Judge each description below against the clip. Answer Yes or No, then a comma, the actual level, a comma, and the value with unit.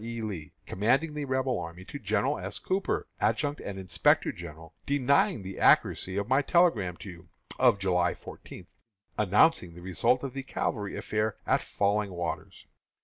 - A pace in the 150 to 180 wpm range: Yes, average, 160 wpm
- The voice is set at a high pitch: No, low, 105 Hz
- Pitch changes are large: Yes, wide, 6.6 semitones